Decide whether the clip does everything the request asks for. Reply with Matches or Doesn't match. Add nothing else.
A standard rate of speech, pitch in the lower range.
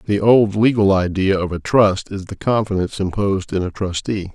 Matches